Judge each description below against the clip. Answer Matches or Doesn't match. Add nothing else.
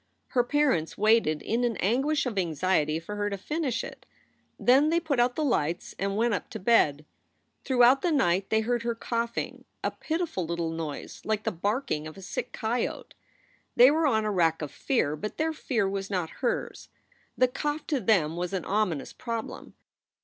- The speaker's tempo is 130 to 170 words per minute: Doesn't match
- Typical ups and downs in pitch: Doesn't match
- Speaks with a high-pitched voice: Matches